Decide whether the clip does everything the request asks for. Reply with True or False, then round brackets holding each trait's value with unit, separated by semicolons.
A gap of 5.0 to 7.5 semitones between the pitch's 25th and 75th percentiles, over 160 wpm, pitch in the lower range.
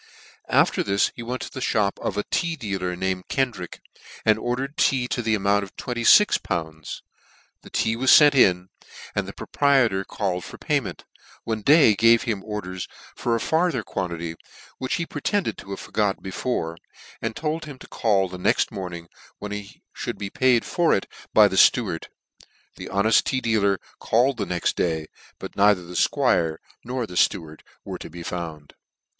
True (5.3 semitones; 175 wpm; 105 Hz)